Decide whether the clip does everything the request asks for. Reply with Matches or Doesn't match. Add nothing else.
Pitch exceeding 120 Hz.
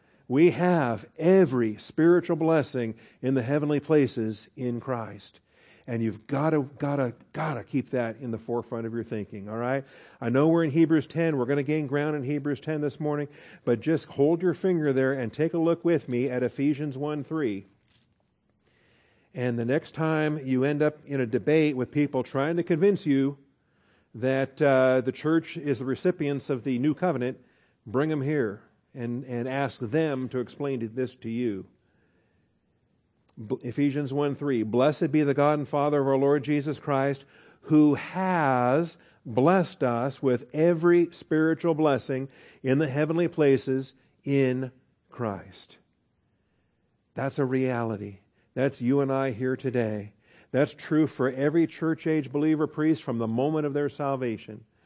Matches